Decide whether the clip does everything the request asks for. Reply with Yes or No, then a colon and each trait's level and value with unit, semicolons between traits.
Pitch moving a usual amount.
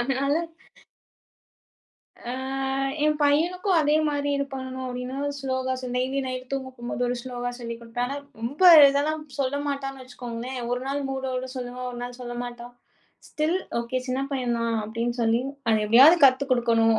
No: narrow, 2.3 semitones